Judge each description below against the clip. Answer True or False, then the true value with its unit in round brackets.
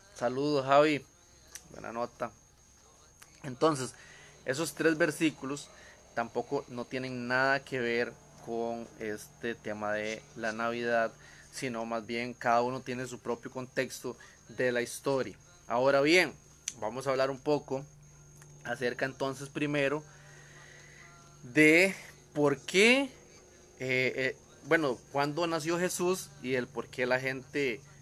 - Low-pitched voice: True (130 Hz)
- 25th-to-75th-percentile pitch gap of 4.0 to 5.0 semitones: False (3.5 semitones)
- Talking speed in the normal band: False (120 wpm)